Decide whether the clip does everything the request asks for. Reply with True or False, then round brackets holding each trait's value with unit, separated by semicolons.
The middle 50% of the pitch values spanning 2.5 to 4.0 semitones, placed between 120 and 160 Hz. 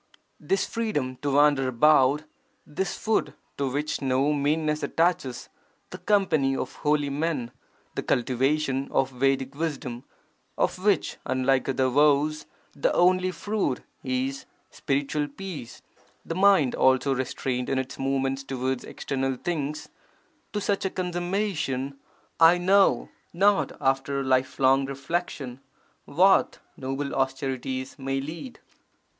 True (3.7 semitones; 140 Hz)